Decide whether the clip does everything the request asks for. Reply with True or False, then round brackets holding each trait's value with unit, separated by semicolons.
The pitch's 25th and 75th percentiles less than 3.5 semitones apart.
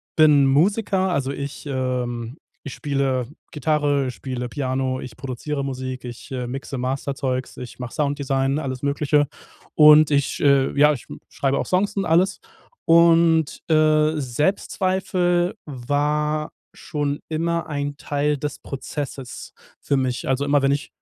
True (2.6 semitones)